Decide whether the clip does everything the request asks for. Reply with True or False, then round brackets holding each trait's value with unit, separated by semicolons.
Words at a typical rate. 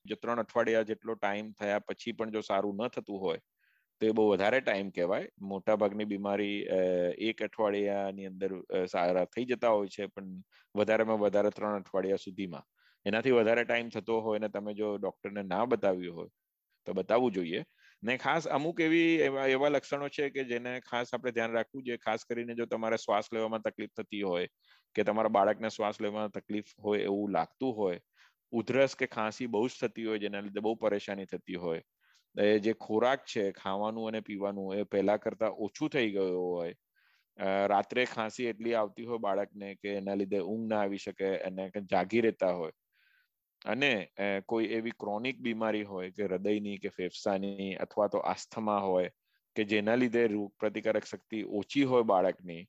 False (175 wpm)